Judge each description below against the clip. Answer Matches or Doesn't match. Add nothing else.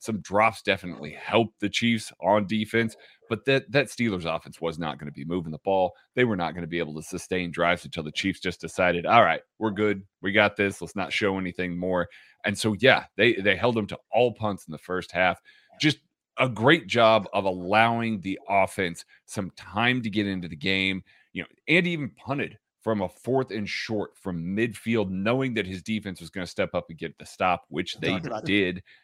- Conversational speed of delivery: Doesn't match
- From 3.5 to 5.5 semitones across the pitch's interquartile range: Matches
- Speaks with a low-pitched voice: Matches